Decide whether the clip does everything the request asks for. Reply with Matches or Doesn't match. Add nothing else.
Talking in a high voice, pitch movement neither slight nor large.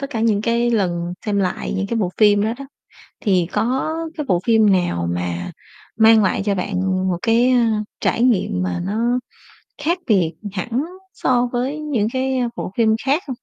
Matches